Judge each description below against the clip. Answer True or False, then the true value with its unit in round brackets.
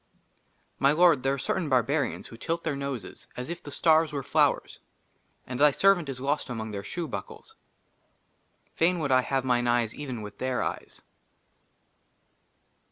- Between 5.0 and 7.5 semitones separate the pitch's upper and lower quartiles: False (4.0 semitones)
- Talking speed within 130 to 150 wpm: False (165 wpm)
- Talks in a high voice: False (135 Hz)